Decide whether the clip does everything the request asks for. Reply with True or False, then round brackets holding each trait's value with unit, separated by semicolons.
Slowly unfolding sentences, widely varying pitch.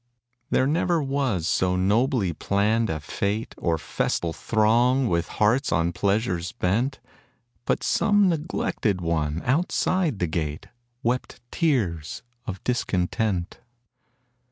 True (110 wpm; 6.8 semitones)